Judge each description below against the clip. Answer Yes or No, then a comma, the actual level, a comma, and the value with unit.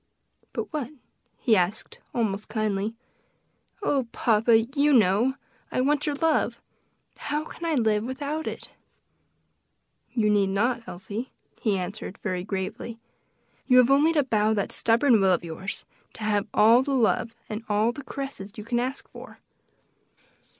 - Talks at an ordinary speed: Yes, average, 150 wpm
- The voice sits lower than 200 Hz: No, high, 225 Hz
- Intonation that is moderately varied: Yes, average, 4.3 semitones